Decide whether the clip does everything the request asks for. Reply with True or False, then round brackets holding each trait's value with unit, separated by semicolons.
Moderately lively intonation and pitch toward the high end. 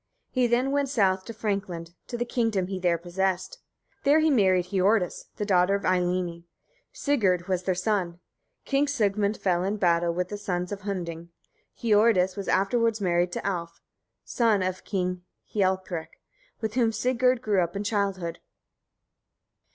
True (3.5 semitones; 195 Hz)